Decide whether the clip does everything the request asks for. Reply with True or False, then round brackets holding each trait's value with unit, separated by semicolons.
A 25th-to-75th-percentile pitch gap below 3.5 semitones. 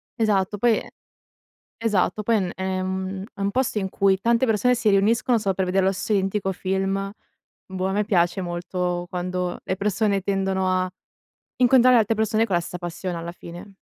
True (2.4 semitones)